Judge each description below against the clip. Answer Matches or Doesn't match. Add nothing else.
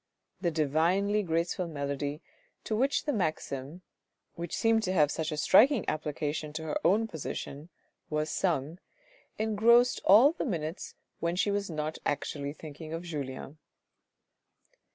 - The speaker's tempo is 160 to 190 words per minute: Doesn't match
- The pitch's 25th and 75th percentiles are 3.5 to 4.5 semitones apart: Doesn't match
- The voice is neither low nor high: Matches